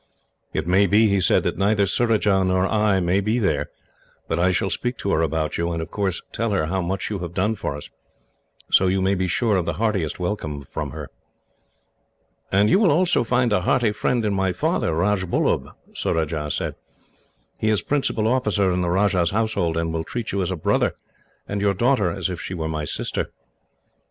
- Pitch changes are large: No, average, 3.7 semitones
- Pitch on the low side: Yes, very low, 95 Hz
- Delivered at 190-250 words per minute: Yes, fast, 205 wpm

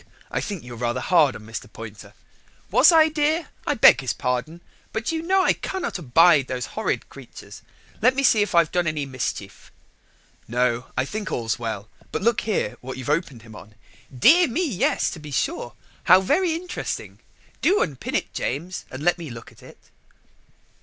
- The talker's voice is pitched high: No, medium, 155 Hz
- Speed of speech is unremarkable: Yes, average, 185 wpm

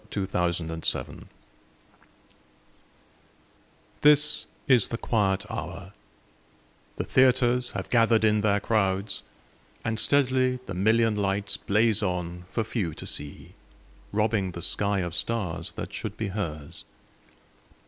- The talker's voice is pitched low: Yes, low, 105 Hz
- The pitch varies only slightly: No, average, 3.7 semitones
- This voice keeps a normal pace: No, slow, 115 wpm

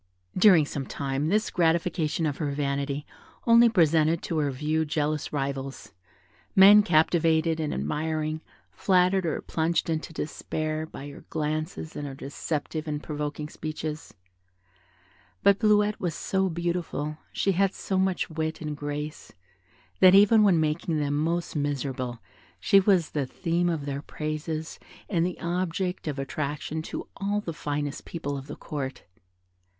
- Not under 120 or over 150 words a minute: Yes, average, 145 wpm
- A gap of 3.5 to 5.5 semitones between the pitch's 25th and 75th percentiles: No, average, 3.0 semitones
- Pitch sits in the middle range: Yes, medium, 155 Hz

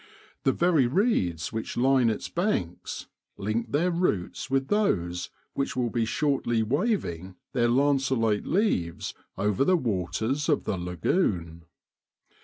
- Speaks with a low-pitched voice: Yes, low, 120 Hz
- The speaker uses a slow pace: Yes, slow, 130 wpm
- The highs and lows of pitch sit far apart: Yes, wide, 7.5 semitones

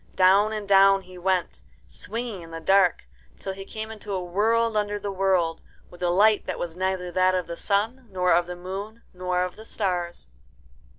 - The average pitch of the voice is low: No, high, 190 Hz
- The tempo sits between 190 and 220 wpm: Yes, average, 195 wpm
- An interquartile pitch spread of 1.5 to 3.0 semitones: Yes, narrow, 2.5 semitones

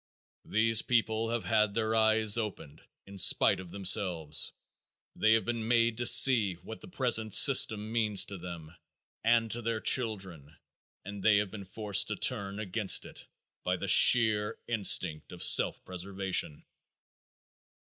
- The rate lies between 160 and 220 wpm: No, average, 150 wpm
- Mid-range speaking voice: No, low, 105 Hz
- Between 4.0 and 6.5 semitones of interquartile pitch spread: No, average, 2.9 semitones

